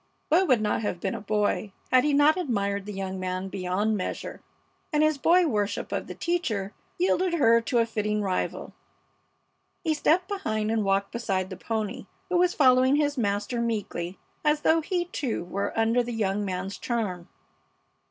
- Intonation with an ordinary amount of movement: No, wide, 6.8 semitones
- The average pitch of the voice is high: Yes, high, 225 Hz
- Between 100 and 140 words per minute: No, average, 175 wpm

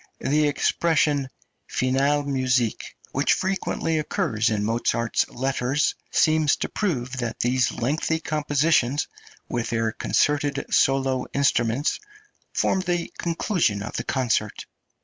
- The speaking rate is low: Yes, slow, 110 wpm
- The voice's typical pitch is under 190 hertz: Yes, low, 135 Hz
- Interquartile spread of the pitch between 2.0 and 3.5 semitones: No, average, 4.1 semitones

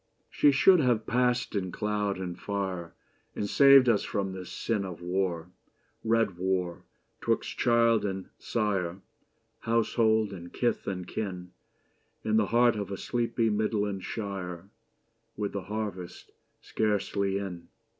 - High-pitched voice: No, low, 100 Hz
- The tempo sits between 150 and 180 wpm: No, average, 140 wpm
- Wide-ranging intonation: No, average, 3.4 semitones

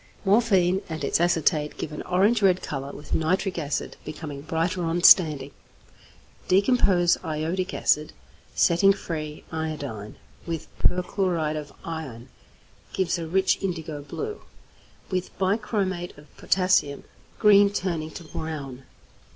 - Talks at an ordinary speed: No, slow, 125 wpm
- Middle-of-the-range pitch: Yes, medium, 170 Hz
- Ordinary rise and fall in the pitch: Yes, average, 3.7 semitones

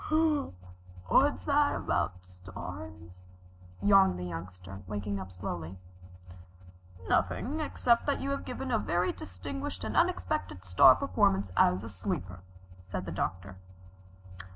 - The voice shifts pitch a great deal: No, narrow, 2.6 semitones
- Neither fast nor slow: No, slow, 120 wpm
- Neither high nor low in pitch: No, very low, 95 Hz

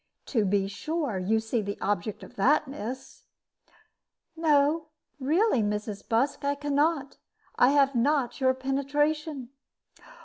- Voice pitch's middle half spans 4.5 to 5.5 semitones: Yes, average, 4.9 semitones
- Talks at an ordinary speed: No, slow, 130 wpm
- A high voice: Yes, very high, 270 Hz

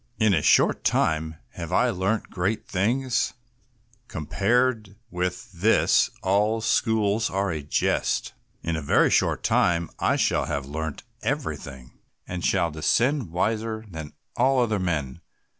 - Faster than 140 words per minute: No, slow, 135 wpm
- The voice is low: Yes, very low, 95 Hz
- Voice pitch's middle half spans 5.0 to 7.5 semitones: Yes, wide, 5.6 semitones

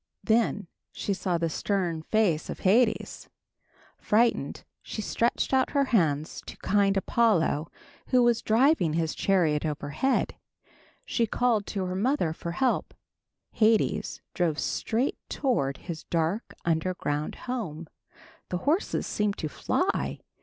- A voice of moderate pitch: No, high, 195 Hz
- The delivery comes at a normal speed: No, slow, 125 wpm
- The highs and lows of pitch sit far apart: Yes, wide, 6.3 semitones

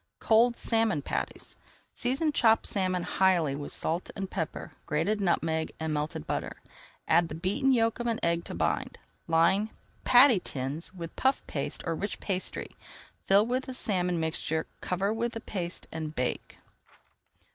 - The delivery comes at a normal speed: Yes, average, 155 wpm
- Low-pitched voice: No, medium, 185 Hz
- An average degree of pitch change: No, wide, 5.8 semitones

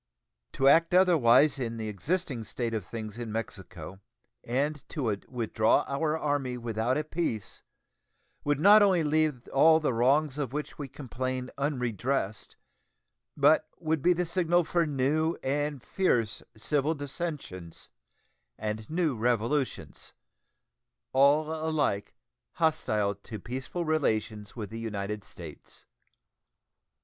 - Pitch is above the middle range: No, low, 135 Hz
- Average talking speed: No, slow, 120 wpm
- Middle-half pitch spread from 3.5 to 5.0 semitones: No, wide, 5.5 semitones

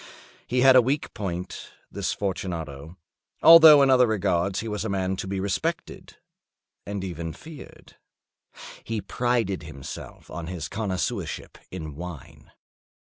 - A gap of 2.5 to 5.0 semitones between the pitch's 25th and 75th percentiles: No, wide, 5.4 semitones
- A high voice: No, very low, 95 Hz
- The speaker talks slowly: Yes, slow, 125 wpm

